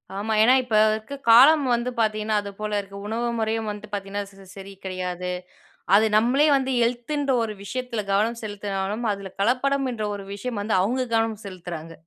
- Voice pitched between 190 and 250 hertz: Yes, high, 215 Hz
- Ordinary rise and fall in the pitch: Yes, average, 3.4 semitones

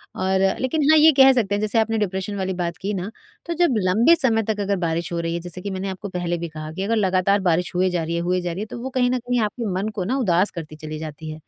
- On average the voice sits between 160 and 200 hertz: Yes, high, 190 Hz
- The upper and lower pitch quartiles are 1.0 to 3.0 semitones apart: No, average, 4.4 semitones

